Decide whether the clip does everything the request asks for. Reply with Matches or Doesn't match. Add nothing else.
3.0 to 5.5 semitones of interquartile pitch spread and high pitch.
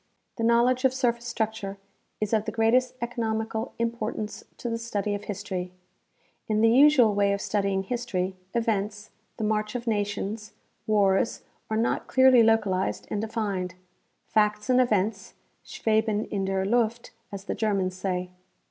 Doesn't match